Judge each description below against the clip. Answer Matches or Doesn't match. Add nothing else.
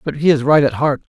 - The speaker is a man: Matches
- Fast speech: Matches